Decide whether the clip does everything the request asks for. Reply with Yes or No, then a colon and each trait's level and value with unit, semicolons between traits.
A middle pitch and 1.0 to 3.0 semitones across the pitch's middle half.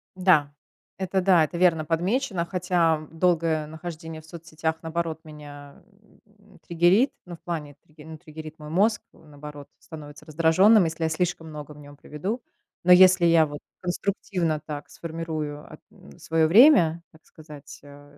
Yes: medium, 160 Hz; average, 2.7 semitones